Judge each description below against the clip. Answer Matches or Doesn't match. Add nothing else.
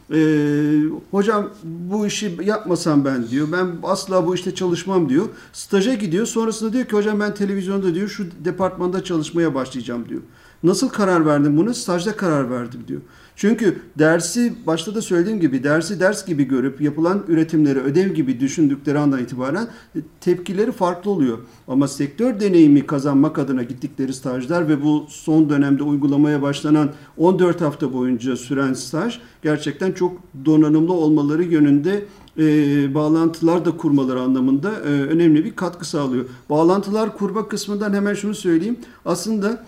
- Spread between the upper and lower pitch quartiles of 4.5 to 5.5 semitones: Matches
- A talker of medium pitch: Matches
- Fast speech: Matches